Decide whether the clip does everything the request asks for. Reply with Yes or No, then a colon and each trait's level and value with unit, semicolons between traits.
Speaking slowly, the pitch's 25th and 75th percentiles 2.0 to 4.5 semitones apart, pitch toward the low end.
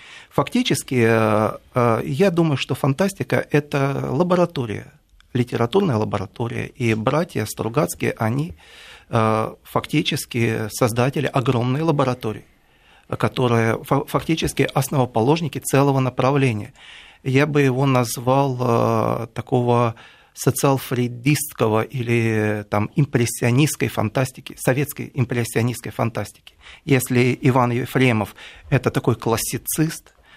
Yes: slow, 80 wpm; average, 3.4 semitones; low, 130 Hz